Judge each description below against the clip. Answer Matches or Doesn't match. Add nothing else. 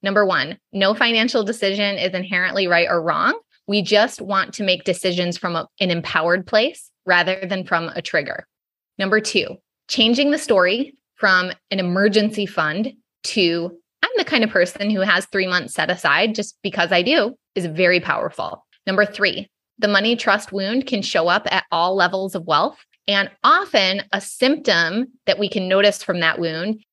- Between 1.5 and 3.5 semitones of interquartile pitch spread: Matches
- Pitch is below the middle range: Doesn't match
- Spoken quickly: Doesn't match